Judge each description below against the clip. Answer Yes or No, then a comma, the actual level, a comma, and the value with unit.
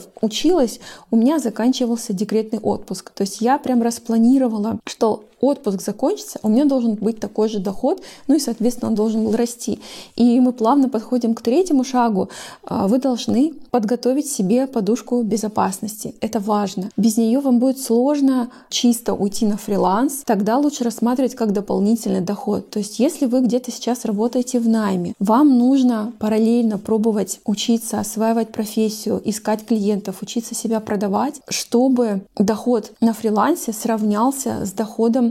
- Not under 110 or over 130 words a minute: No, average, 145 wpm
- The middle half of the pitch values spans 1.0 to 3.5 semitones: Yes, narrow, 2.5 semitones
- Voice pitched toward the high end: Yes, high, 230 Hz